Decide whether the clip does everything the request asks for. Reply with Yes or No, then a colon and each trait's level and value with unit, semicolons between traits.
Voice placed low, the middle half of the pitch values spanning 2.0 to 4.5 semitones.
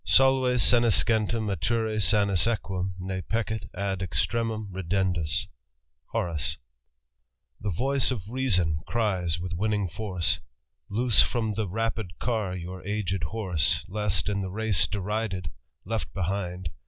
Yes: low, 100 Hz; average, 3.7 semitones